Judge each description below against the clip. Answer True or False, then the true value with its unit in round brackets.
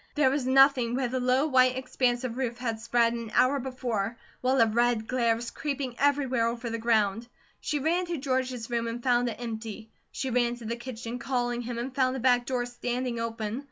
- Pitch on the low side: False (245 Hz)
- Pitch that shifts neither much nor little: False (1.9 semitones)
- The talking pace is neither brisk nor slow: False (210 wpm)